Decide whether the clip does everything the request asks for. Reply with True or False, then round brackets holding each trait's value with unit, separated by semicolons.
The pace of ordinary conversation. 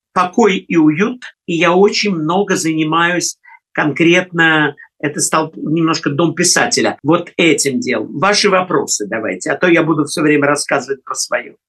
True (150 wpm)